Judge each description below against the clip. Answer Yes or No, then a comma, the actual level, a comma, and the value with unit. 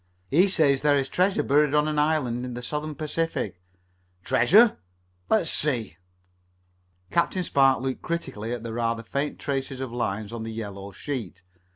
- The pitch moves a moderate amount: Yes, average, 4.6 semitones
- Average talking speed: Yes, average, 165 wpm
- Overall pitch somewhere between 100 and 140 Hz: Yes, low, 135 Hz